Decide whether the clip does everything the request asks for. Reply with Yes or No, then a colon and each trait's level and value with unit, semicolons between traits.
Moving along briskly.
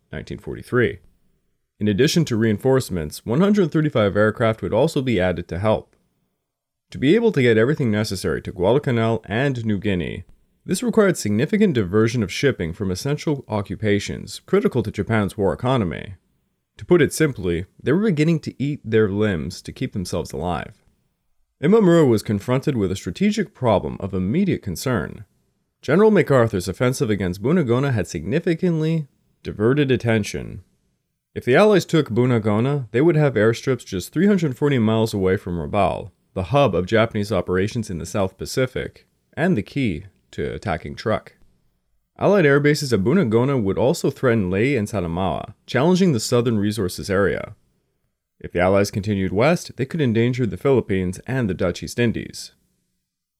No: average, 150 wpm